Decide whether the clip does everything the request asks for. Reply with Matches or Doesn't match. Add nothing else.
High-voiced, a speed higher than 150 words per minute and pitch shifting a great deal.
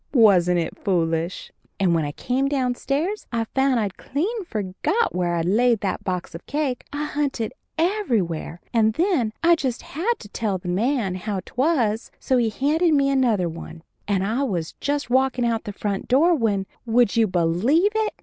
Matches